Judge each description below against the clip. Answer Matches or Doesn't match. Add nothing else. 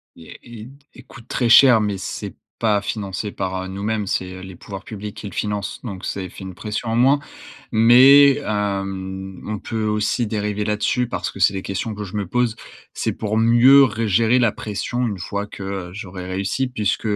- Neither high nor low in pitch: Doesn't match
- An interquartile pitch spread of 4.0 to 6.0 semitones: Doesn't match